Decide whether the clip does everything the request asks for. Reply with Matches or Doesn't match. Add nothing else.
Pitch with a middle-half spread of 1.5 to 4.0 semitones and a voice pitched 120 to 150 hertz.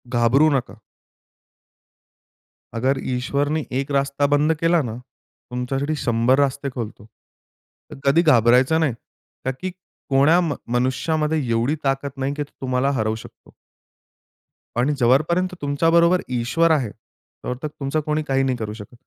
Matches